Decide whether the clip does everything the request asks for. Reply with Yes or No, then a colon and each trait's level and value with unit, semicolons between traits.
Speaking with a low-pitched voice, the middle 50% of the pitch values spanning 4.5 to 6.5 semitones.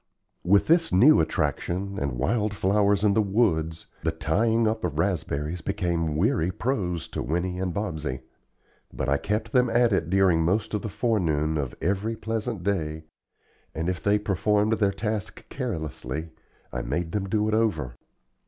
Yes: very low, 95 Hz; average, 5.0 semitones